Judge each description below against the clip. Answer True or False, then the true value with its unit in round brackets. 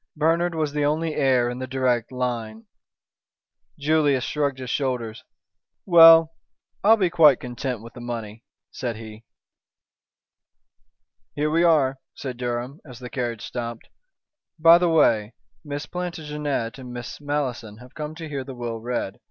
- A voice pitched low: True (130 Hz)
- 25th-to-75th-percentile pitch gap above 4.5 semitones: False (4.1 semitones)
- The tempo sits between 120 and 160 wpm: True (145 wpm)